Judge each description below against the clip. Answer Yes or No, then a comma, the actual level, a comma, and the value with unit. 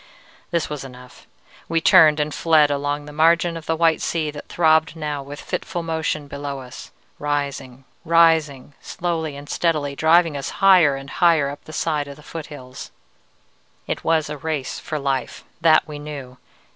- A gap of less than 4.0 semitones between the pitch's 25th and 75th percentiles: Yes, narrow, 2.4 semitones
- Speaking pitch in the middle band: Yes, medium, 150 Hz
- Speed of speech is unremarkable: Yes, average, 170 wpm